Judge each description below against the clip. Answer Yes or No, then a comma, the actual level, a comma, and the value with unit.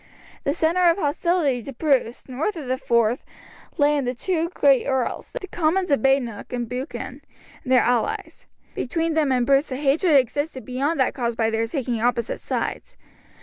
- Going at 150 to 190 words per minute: Yes, average, 180 wpm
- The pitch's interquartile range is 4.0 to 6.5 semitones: Yes, average, 4.3 semitones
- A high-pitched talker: Yes, very high, 270 Hz